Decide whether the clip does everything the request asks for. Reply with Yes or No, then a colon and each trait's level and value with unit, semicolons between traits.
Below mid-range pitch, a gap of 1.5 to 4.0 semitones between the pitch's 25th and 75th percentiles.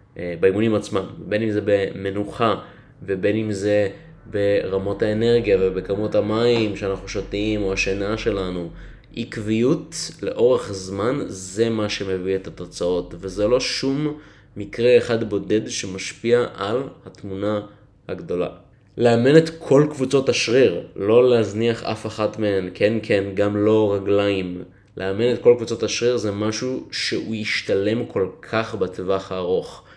Yes: low, 105 Hz; average, 3.1 semitones